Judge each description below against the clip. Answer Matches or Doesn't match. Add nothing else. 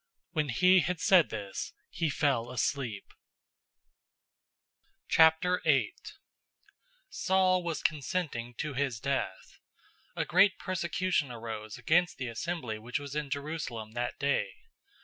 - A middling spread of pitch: Doesn't match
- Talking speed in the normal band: Doesn't match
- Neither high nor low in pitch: Matches